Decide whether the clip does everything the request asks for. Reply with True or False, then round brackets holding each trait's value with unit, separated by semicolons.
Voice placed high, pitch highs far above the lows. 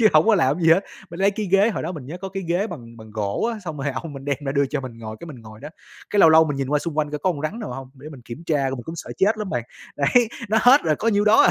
False (155 Hz; 6.3 semitones)